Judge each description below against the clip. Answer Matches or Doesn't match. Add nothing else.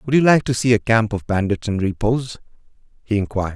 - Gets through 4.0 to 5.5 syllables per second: Doesn't match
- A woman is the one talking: Doesn't match